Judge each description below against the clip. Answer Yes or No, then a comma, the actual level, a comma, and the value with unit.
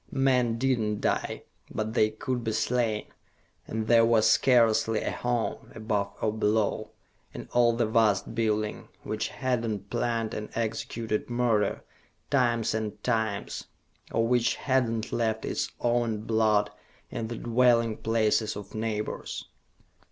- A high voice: No, low, 115 Hz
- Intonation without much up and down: Yes, narrow, 1.6 semitones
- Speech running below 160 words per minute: Yes, average, 140 wpm